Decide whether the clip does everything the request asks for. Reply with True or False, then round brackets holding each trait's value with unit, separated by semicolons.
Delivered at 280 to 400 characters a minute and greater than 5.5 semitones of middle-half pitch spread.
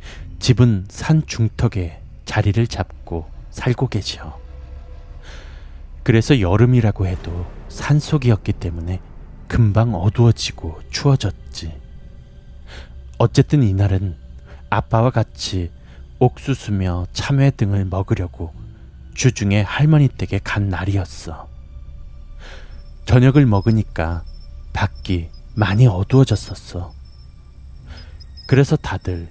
False (210 characters per minute; 8.1 semitones)